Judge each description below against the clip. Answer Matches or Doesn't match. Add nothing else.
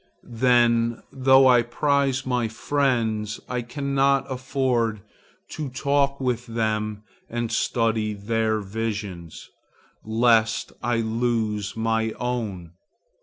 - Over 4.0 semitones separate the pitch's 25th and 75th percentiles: Doesn't match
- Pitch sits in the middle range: Doesn't match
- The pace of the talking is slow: Matches